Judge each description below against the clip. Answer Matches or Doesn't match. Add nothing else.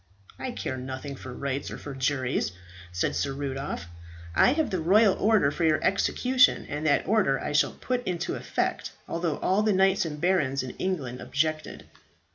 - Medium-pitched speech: Matches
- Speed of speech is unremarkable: Matches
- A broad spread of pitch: Matches